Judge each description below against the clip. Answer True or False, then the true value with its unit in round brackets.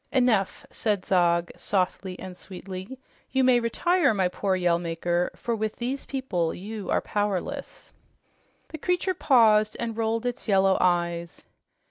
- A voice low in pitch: False (205 Hz)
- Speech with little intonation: False (4.7 semitones)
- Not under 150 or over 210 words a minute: False (140 wpm)